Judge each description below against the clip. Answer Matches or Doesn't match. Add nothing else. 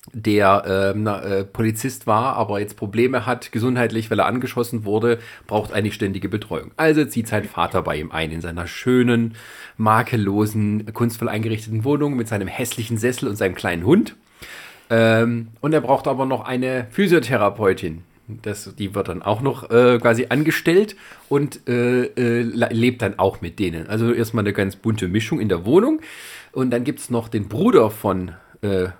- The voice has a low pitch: Matches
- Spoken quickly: Doesn't match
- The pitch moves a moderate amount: Matches